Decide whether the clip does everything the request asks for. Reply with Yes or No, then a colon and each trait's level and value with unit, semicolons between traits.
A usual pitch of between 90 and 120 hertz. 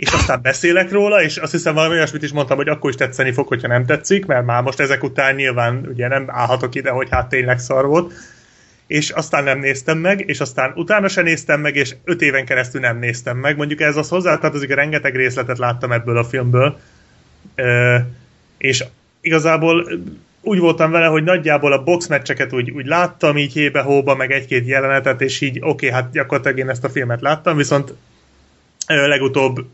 No: medium, 140 Hz